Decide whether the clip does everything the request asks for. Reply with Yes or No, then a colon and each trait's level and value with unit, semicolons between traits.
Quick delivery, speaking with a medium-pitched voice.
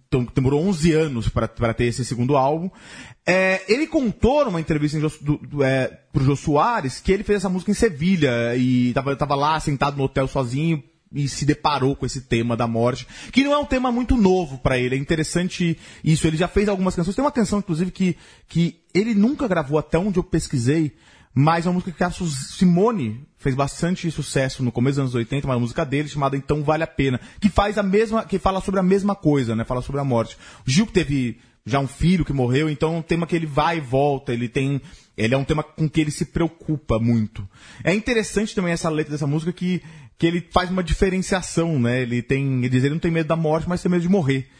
Yes: fast, 225 wpm; medium, 155 Hz